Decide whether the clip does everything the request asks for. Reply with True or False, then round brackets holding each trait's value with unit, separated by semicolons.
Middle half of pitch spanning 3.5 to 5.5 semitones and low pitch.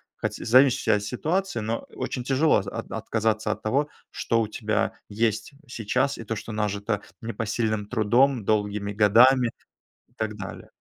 False (2.9 semitones; 110 Hz)